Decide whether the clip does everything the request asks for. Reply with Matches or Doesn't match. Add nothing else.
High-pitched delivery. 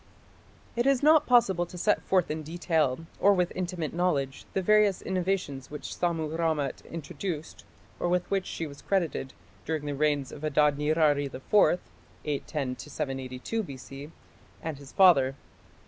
Doesn't match